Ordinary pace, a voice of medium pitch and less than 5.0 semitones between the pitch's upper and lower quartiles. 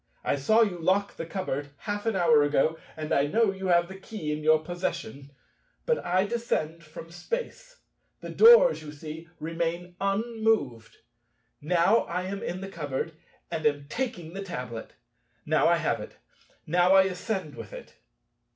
Yes: average, 165 wpm; medium, 175 Hz; average, 4.5 semitones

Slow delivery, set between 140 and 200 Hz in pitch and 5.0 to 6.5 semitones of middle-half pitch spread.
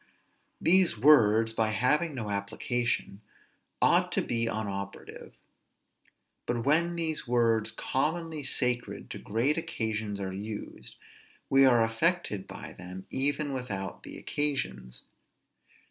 No: slow, 110 wpm; low, 115 Hz; wide, 5.4 semitones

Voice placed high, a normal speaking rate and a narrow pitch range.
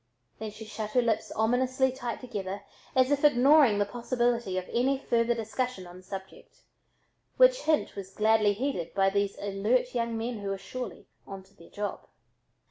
No: high, 225 Hz; average, 170 wpm; average, 4.0 semitones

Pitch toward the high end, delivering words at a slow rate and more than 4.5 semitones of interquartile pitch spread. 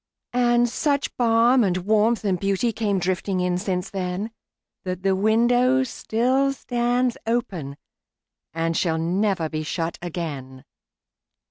Yes: high, 200 Hz; slow, 110 wpm; average, 5.0 semitones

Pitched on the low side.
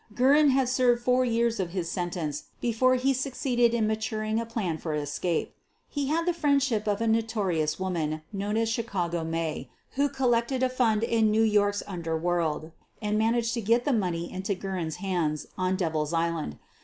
No: high, 215 Hz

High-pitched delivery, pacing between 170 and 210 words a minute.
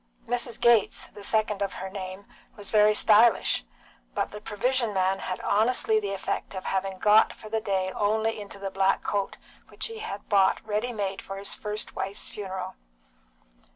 Yes: high, 205 Hz; average, 175 wpm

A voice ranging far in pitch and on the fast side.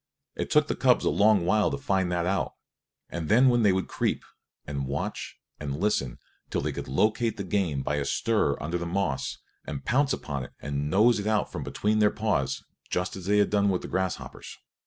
Yes: wide, 6.2 semitones; fast, 210 wpm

